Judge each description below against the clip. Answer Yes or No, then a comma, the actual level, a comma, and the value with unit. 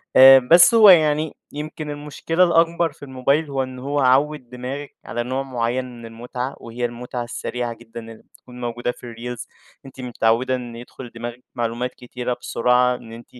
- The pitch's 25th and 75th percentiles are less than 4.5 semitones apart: Yes, average, 2.8 semitones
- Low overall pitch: Yes, low, 125 Hz